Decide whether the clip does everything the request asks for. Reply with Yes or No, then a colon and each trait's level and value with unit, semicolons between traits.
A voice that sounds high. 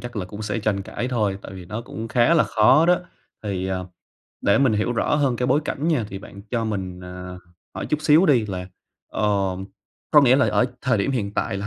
No: low, 110 Hz